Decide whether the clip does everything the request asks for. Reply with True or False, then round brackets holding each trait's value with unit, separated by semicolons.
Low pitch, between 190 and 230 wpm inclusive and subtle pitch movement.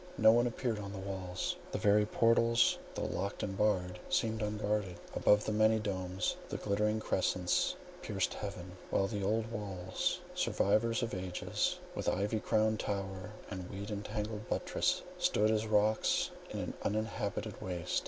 False (105 Hz; 155 wpm; 2.1 semitones)